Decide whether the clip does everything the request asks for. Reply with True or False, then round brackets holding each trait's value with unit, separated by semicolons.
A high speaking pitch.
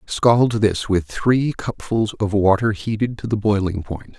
False (105 Hz)